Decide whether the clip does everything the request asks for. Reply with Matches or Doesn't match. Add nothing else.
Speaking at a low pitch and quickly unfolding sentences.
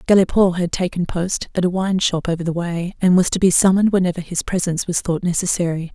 Doesn't match